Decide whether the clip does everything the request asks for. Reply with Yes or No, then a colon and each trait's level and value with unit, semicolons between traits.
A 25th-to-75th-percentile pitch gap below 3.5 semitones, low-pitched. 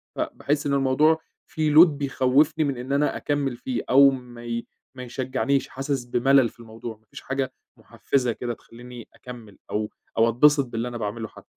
Yes: average, 2.8 semitones; low, 130 Hz